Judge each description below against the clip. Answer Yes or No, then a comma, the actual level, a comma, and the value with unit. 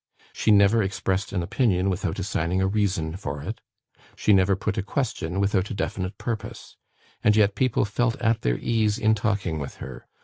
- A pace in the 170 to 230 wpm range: Yes, average, 180 wpm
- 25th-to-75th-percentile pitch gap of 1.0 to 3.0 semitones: Yes, average, 2.7 semitones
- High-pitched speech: No, low, 100 Hz